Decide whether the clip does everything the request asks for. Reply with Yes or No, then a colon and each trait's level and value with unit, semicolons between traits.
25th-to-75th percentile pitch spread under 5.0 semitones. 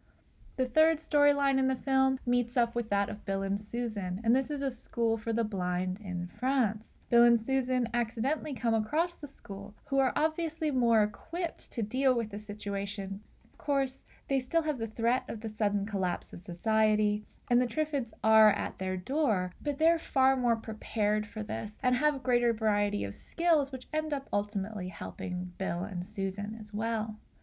Yes: average, 4.6 semitones